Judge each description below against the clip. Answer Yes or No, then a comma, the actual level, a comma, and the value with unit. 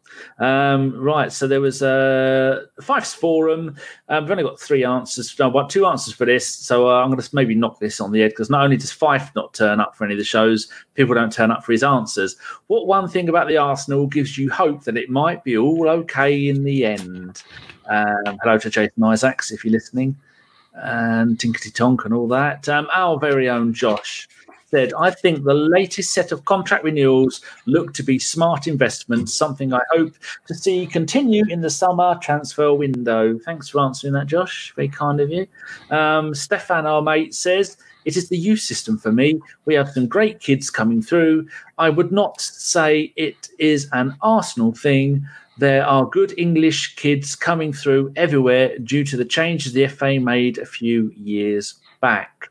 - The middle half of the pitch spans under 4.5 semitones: No, average, 4.9 semitones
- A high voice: No, medium, 140 Hz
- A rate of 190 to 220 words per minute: Yes, average, 195 wpm